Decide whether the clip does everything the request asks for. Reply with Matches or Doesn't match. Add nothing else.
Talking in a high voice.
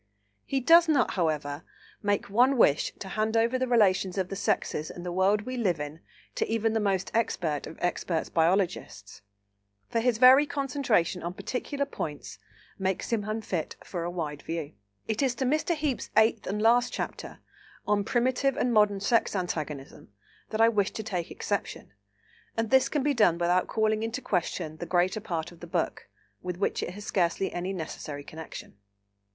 Matches